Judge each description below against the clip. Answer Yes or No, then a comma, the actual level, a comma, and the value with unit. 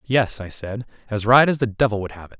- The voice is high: No, low, 110 Hz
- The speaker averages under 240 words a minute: No, fast, 275 wpm